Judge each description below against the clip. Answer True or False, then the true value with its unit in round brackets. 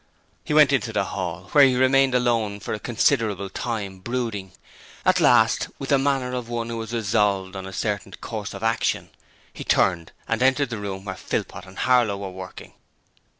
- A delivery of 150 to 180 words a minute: False (190 wpm)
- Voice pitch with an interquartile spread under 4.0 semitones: False (4.6 semitones)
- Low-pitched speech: True (115 Hz)